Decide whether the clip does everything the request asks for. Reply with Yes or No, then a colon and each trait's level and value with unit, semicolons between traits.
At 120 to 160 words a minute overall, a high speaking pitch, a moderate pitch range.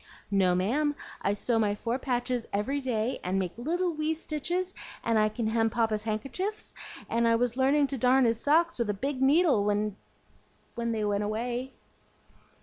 No: average, 175 wpm; high, 235 Hz; average, 4.7 semitones